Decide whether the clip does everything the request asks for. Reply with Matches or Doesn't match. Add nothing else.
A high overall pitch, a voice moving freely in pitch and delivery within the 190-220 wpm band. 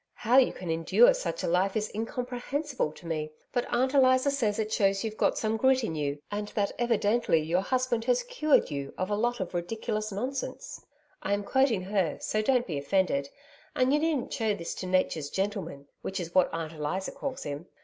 Matches